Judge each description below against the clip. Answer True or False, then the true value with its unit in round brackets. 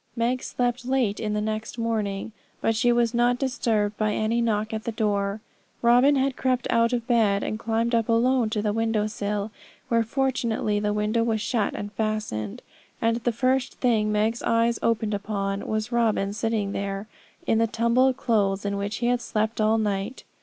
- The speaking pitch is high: True (225 Hz)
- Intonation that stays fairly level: True (2.1 semitones)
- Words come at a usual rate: True (180 wpm)